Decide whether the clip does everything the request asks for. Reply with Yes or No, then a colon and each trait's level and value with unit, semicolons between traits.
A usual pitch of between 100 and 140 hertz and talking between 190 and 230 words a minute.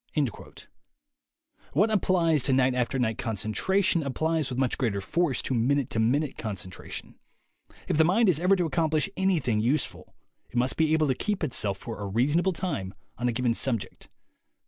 No: low, 135 Hz; average, 170 wpm